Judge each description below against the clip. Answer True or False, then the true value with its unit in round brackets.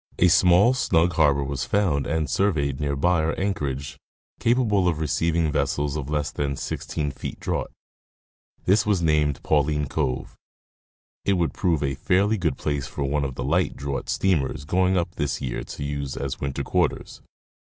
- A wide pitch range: False (4.2 semitones)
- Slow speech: False (170 wpm)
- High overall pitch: False (75 Hz)